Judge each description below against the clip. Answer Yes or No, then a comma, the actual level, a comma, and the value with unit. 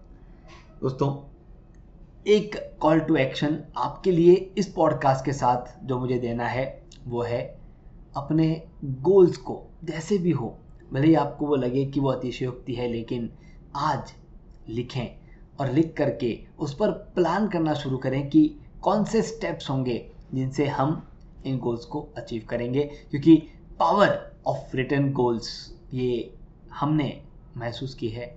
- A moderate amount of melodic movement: Yes, average, 4.1 semitones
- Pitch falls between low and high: Yes, medium, 145 Hz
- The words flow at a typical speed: Yes, average, 140 wpm